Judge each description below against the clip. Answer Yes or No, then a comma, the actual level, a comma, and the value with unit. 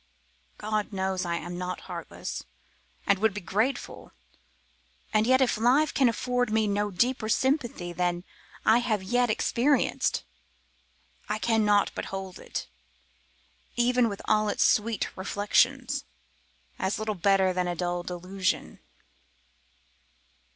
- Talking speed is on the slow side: Yes, slow, 125 wpm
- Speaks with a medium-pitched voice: No, high, 210 Hz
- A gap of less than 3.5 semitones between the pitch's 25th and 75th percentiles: No, average, 4.2 semitones